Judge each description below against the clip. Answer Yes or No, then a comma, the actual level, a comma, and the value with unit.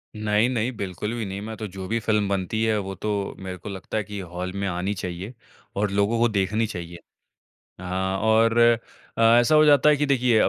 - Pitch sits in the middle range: No, low, 105 Hz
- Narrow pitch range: No, average, 3.0 semitones